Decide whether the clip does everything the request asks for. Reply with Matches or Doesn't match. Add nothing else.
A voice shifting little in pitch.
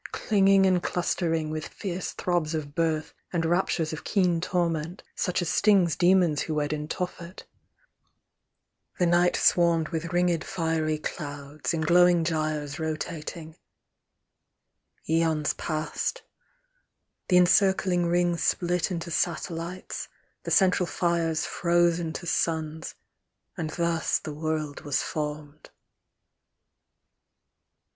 Matches